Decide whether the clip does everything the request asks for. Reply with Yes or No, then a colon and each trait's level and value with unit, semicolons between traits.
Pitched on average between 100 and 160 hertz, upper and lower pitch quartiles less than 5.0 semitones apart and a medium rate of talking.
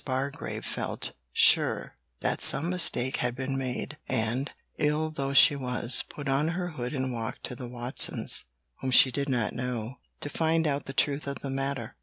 Yes: low, 135 Hz; narrow, 2.6 semitones; average, 180 wpm